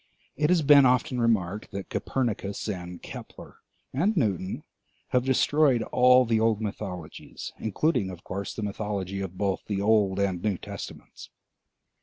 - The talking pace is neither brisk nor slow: Yes, average, 145 wpm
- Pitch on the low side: Yes, low, 105 Hz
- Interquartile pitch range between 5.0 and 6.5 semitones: No, average, 4.6 semitones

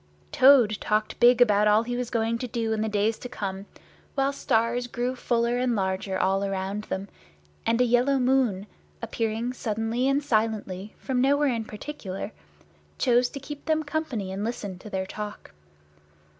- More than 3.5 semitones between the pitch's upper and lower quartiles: No, average, 3.2 semitones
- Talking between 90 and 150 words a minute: No, average, 170 wpm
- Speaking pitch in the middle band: No, high, 230 Hz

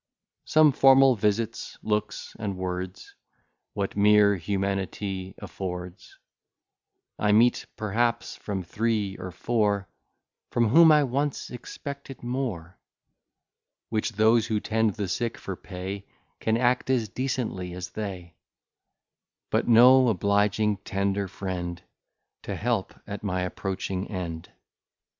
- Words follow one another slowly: Yes, slow, 115 wpm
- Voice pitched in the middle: No, low, 105 Hz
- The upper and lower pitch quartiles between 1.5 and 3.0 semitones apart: No, average, 3.7 semitones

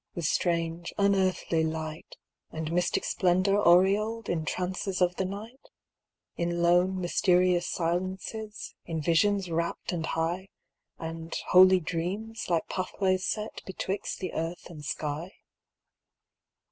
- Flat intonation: Yes, narrow, 2.3 semitones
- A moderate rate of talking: No, slow, 120 wpm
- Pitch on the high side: No, medium, 180 Hz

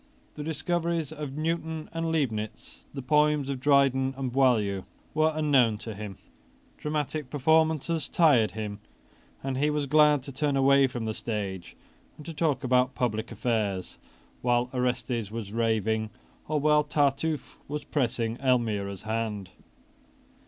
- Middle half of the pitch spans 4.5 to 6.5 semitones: Yes, average, 5.0 semitones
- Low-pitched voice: Yes, low, 130 Hz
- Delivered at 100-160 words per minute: Yes, average, 140 wpm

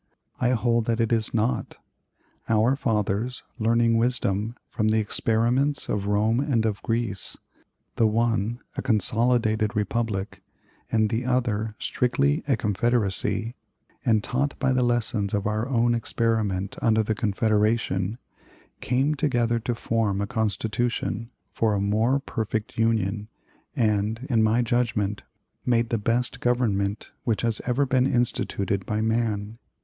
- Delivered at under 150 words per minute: Yes, slow, 135 wpm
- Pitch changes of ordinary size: No, narrow, 2.2 semitones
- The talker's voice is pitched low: Yes, low, 115 Hz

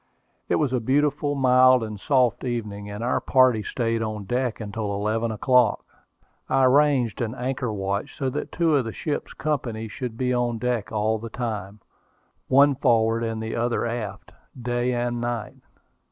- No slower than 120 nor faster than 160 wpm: No, average, 170 wpm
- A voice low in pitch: Yes, low, 120 Hz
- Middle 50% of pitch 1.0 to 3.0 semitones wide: Yes, average, 2.7 semitones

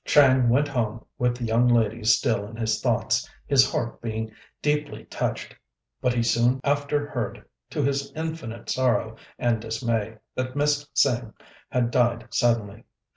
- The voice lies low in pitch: Yes, low, 120 Hz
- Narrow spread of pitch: No, average, 3.4 semitones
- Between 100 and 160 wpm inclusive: Yes, average, 150 wpm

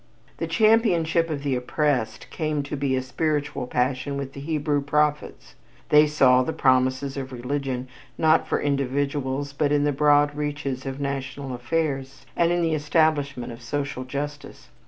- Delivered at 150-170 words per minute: Yes, average, 155 wpm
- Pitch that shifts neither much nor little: No, narrow, 2.2 semitones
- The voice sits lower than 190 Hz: Yes, medium, 140 Hz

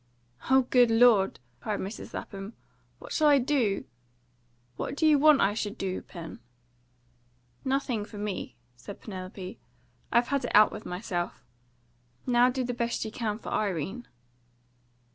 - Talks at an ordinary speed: Yes, average, 145 wpm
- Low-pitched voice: No, high, 220 Hz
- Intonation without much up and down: No, average, 4.1 semitones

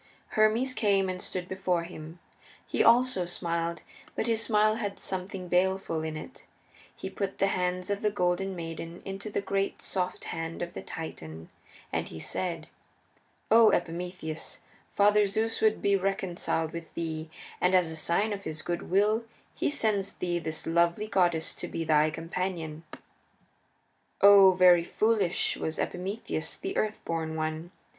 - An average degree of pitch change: Yes, average, 3.3 semitones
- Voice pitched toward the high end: No, medium, 180 Hz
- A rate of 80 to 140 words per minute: No, average, 155 wpm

